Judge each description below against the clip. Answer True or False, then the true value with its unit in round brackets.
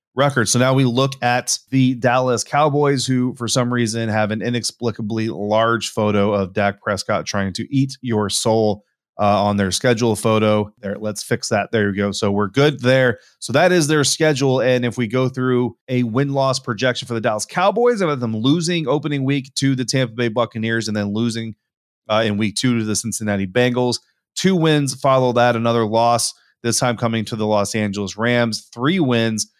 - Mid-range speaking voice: False (120 Hz)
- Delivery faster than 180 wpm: True (200 wpm)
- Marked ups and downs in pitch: False (3.3 semitones)